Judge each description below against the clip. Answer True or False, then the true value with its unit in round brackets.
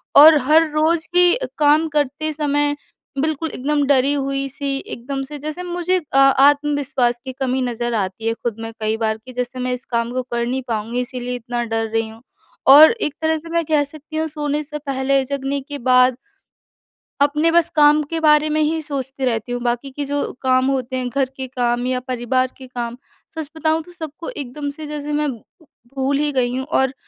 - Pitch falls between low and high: False (275 Hz)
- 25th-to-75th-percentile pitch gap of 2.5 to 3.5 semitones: True (3.2 semitones)